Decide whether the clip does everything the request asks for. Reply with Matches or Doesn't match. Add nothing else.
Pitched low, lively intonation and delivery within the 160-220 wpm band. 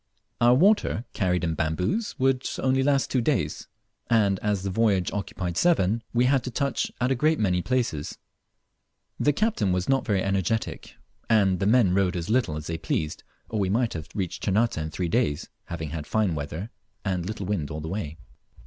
Matches